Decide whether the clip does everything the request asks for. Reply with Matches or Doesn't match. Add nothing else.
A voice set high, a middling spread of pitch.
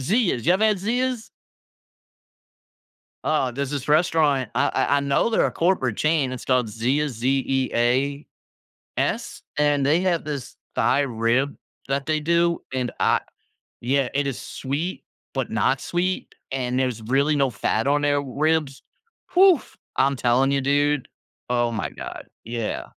Doesn't match